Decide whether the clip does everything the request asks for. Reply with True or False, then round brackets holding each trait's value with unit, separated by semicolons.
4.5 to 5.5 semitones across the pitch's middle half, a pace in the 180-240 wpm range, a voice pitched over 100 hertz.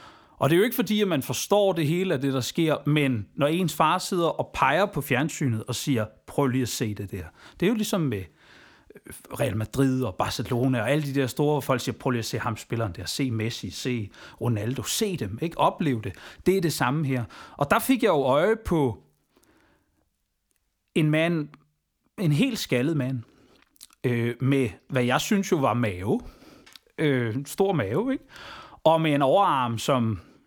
True (5.1 semitones; 195 wpm; 135 Hz)